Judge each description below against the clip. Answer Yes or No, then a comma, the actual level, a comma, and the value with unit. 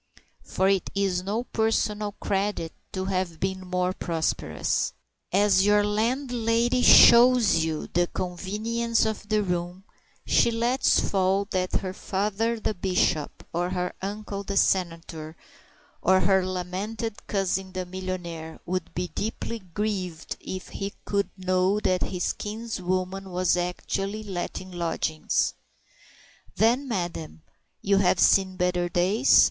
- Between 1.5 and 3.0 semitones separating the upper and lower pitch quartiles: Yes, average, 2.7 semitones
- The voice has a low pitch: No, high, 190 Hz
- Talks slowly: Yes, slow, 125 wpm